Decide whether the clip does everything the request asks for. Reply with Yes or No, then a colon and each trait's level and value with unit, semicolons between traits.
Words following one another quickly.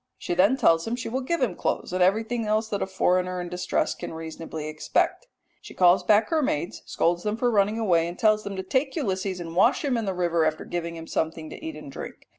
Yes: fast, 240 wpm